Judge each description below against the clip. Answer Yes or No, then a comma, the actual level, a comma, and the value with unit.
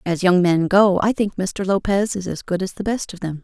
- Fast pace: Yes, fast, 280 wpm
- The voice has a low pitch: No, high, 190 Hz